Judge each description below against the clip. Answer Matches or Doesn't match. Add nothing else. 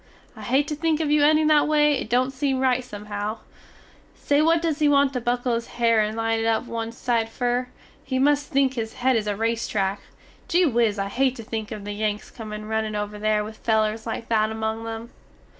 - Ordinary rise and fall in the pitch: Matches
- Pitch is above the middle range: Matches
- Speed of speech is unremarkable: Doesn't match